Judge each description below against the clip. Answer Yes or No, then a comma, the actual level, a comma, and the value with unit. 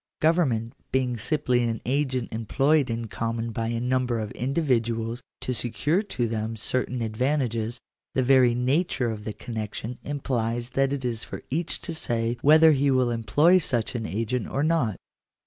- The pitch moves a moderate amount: Yes, average, 3.2 semitones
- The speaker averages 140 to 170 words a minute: Yes, average, 165 wpm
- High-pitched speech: No, low, 125 Hz